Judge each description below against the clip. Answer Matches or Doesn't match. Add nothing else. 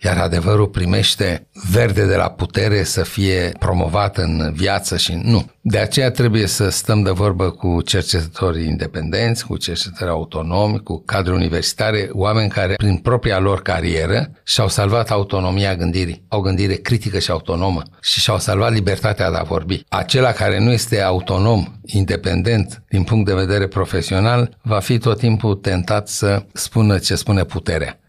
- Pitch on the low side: Matches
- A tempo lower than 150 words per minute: Doesn't match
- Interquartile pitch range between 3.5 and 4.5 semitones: Doesn't match